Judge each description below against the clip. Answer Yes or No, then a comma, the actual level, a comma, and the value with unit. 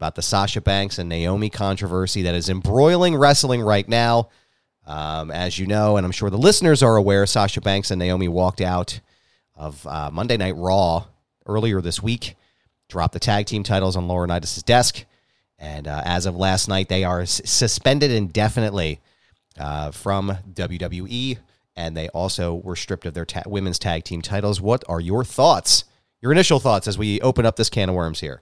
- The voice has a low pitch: Yes, low, 100 Hz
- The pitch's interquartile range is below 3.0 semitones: No, average, 3.7 semitones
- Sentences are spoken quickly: No, average, 185 wpm